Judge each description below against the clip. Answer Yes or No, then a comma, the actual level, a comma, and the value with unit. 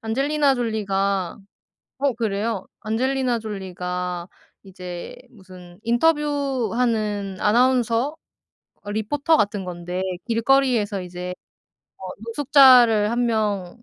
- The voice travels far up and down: No, average, 4.7 semitones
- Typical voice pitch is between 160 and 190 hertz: No, high, 220 Hz